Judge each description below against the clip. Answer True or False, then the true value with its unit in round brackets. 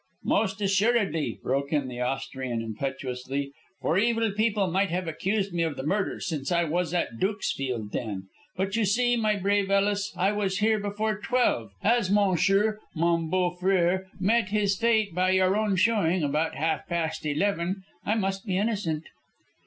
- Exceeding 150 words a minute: True (165 wpm)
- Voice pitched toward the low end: False (190 Hz)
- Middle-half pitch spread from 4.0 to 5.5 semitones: True (4.5 semitones)